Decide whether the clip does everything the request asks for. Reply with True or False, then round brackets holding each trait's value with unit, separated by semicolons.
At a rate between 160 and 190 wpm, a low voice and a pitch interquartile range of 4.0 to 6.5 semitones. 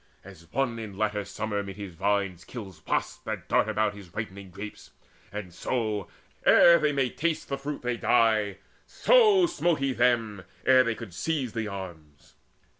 True (170 wpm; 110 Hz; 4.5 semitones)